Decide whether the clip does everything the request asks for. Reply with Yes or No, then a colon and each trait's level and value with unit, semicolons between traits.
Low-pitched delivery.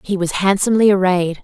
No: high, 190 Hz